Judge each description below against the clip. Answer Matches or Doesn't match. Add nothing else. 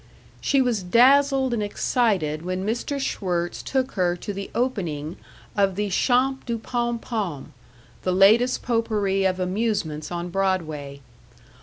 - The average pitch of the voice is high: Matches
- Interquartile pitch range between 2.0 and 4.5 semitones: Doesn't match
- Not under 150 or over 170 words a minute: Doesn't match